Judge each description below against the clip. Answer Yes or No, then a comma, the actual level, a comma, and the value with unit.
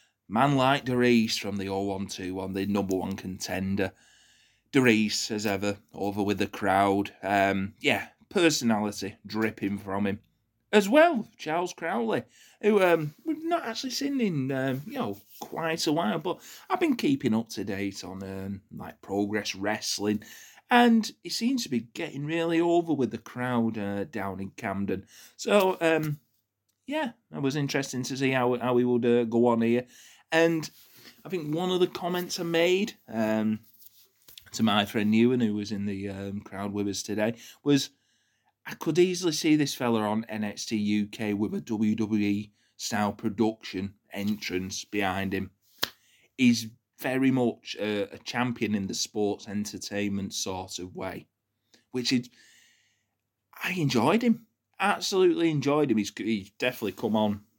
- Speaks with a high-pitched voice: No, low, 115 Hz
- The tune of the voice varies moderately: No, wide, 6.5 semitones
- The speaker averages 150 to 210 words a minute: Yes, average, 155 wpm